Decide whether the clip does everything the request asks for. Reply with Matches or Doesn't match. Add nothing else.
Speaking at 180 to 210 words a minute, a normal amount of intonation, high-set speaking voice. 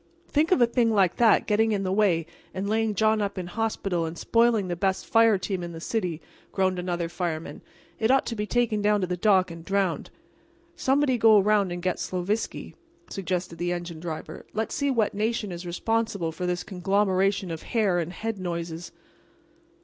Matches